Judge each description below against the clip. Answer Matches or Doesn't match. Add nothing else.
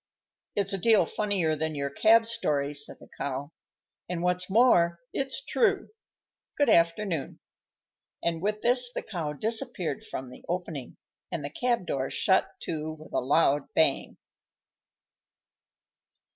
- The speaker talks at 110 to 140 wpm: Matches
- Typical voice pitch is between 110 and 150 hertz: Doesn't match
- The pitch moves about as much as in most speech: Doesn't match